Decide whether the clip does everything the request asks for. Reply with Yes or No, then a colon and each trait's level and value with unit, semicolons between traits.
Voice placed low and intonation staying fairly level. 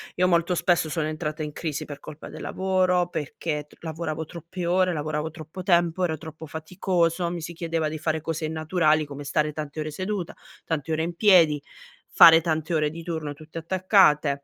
No: medium, 160 Hz; narrow, 2.1 semitones